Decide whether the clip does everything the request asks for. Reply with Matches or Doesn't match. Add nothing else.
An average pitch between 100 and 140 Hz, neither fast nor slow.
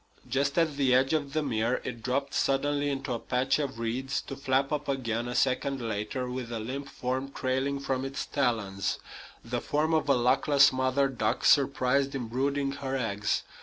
Matches